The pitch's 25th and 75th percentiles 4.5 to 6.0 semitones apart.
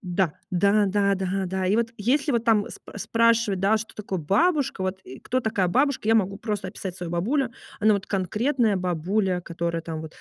No: average, 3.8 semitones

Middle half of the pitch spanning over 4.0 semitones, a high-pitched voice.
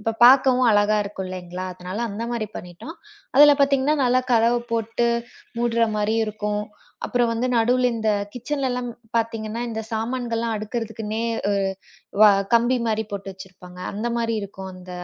No: average, 2.7 semitones; high, 225 Hz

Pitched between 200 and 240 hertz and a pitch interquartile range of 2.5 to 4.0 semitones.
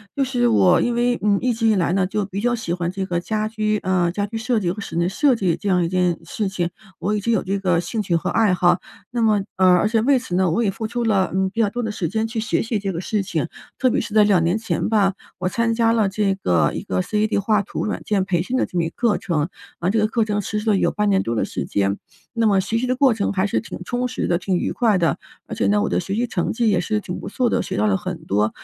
Yes: high, 205 Hz; average, 3.6 semitones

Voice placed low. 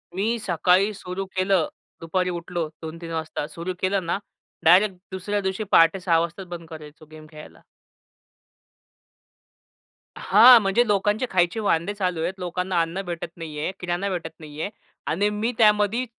No: medium, 180 Hz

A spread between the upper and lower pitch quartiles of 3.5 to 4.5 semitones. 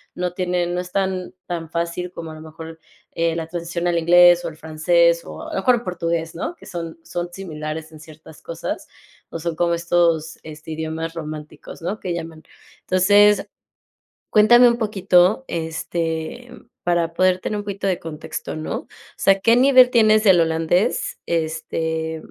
No: narrow, 2.4 semitones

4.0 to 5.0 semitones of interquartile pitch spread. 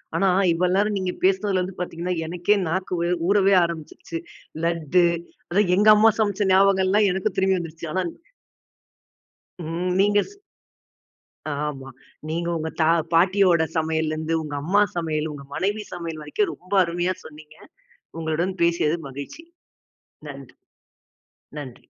No: average, 3.4 semitones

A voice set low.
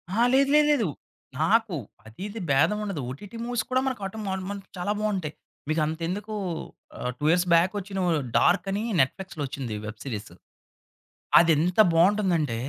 No: medium, 185 Hz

